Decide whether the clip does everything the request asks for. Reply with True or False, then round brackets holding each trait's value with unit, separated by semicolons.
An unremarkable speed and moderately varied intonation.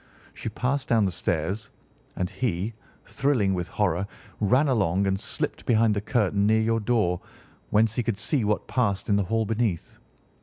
True (175 wpm; 3.0 semitones)